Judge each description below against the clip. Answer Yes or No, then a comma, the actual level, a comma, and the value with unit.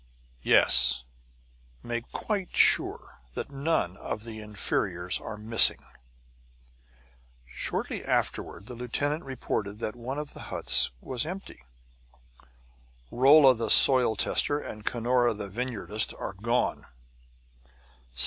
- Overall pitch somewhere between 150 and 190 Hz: No, low, 120 Hz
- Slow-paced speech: Yes, slow, 110 wpm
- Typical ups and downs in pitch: Yes, average, 4.0 semitones